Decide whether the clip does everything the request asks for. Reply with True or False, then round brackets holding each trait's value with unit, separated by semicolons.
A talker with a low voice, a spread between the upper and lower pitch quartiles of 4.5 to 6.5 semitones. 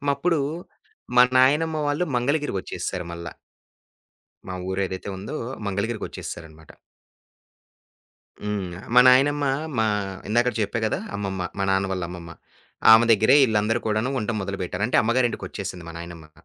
True (105 Hz; 5.1 semitones)